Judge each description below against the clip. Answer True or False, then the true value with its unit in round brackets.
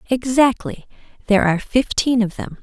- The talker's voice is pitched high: True (235 Hz)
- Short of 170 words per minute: True (135 wpm)